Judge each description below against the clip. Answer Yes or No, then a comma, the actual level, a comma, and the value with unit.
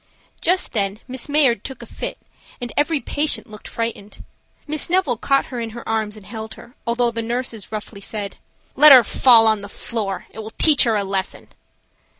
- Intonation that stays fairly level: No, average, 3.8 semitones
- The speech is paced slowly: No, average, 195 wpm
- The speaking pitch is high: Yes, high, 230 Hz